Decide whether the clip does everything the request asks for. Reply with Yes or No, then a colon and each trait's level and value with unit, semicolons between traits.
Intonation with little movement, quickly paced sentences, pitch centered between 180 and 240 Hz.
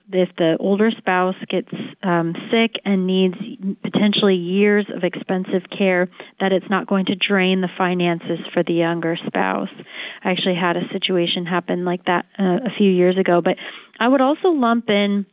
No: narrow, 2.3 semitones; average, 175 wpm; medium, 185 Hz